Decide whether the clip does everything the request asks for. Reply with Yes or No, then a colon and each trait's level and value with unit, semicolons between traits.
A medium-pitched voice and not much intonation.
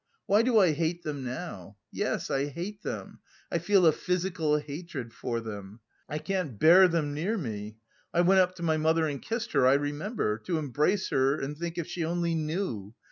No: medium, 160 Hz; average, 4.7 semitones